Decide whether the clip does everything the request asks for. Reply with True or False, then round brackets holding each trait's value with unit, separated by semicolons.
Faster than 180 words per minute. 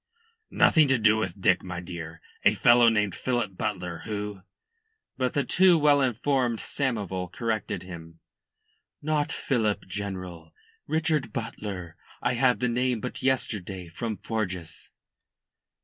False (135 wpm)